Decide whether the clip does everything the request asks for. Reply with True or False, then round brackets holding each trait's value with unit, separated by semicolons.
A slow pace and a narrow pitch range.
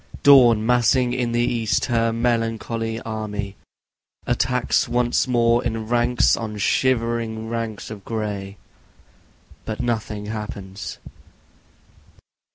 True (100 wpm; 1.8 semitones)